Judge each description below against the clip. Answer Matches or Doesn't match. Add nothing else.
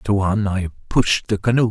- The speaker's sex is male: Matches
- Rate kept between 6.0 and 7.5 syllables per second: Doesn't match